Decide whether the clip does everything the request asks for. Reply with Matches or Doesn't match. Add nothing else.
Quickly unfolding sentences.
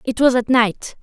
Matches